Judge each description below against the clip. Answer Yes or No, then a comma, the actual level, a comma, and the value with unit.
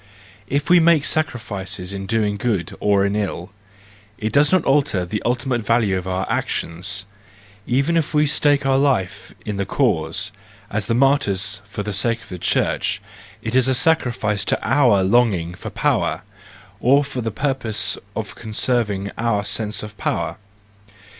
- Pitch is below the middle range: Yes, low, 110 Hz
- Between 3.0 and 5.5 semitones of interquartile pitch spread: Yes, average, 5.2 semitones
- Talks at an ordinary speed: Yes, average, 160 wpm